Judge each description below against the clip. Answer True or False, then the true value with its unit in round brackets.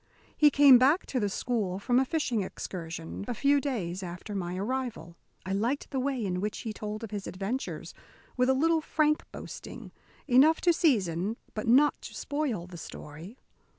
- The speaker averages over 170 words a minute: True (180 wpm)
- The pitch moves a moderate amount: False (6.4 semitones)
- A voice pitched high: True (230 Hz)